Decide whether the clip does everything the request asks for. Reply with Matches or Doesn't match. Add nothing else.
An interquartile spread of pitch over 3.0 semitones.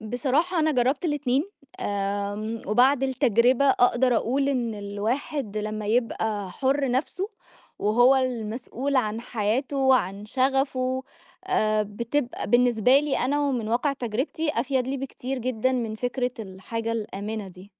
Matches